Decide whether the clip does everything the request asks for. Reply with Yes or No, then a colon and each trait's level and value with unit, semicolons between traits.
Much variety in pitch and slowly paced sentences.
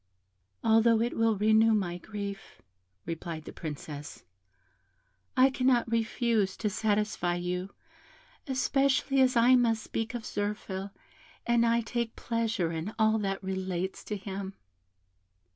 No: average, 3.4 semitones; slow, 125 wpm